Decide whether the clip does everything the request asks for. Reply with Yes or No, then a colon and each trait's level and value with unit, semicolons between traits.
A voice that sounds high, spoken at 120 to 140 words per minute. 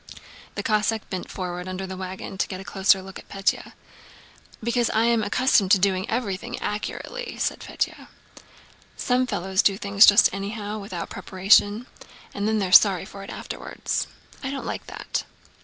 No: high, 200 Hz; average, 170 wpm